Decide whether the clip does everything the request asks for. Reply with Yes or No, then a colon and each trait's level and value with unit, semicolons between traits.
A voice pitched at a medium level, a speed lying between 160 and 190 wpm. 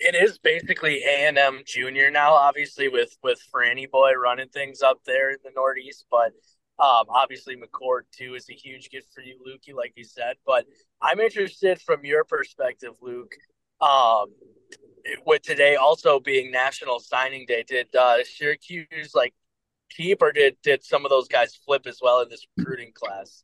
Yes: medium, 145 Hz; average, 175 wpm